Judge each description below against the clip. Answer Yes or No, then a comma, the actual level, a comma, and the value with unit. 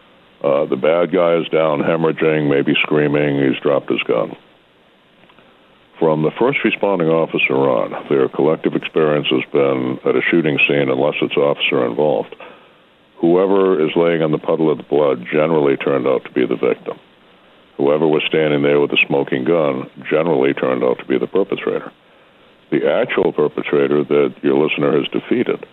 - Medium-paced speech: Yes, average, 165 wpm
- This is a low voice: Yes, very low, 75 Hz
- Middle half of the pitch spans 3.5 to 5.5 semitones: No, average, 3.0 semitones